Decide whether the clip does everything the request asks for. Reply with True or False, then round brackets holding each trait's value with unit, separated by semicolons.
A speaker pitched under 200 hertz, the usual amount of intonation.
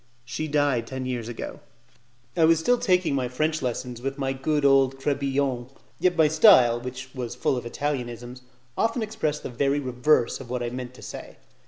True (135 Hz; 3.4 semitones)